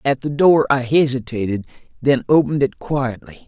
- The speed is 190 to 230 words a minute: No, average, 155 wpm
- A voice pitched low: Yes, low, 130 Hz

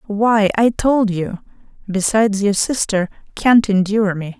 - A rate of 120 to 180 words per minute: Yes, slow, 135 wpm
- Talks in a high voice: Yes, high, 205 Hz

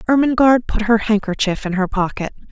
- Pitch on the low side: No, high, 220 Hz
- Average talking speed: Yes, average, 165 wpm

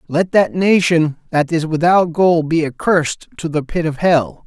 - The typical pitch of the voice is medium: Yes, medium, 165 Hz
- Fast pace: No, average, 190 wpm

